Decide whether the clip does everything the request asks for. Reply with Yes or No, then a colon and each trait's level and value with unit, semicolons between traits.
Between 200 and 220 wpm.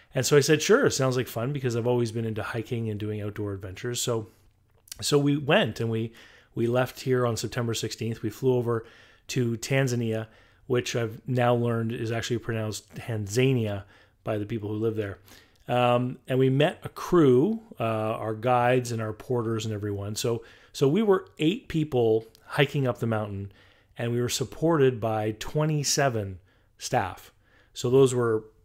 No: average, 175 wpm